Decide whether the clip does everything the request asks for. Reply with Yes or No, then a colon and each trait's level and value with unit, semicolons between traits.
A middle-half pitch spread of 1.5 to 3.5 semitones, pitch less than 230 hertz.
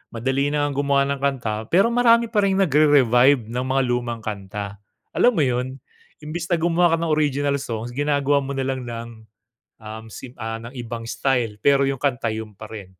No: average, 4.0 semitones; low, 135 Hz